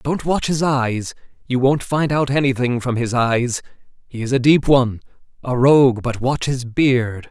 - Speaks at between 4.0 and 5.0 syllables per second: Yes, 4.5 syllables/s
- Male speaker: Yes, male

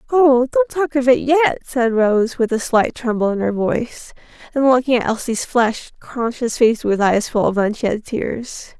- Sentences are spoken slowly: No, average, 190 wpm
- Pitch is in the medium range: No, high, 245 Hz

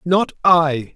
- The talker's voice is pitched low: No, medium, 160 Hz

